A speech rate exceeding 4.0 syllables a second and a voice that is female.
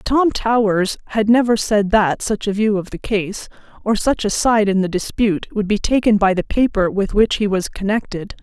Yes: 4.9 syllables/s; female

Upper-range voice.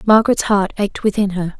Yes: high, 200 Hz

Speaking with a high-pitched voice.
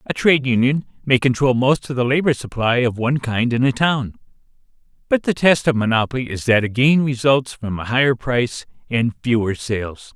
No: low, 125 Hz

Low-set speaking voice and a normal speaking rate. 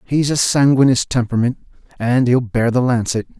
Yes: low, 125 Hz; average, 160 wpm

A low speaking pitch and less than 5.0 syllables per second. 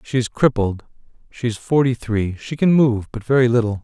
No: low, 120 Hz; 5.2 syllables/s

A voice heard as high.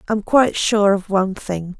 Yes: high, 200 Hz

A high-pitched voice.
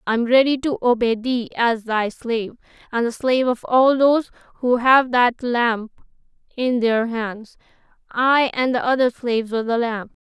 Yes: high, 240 Hz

